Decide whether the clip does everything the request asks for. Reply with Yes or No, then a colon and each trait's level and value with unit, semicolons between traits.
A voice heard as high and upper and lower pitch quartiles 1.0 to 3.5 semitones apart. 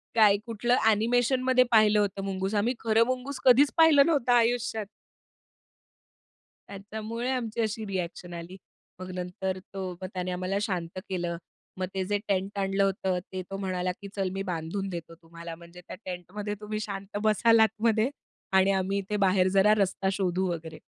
Yes: high, 195 Hz; average, 3.1 semitones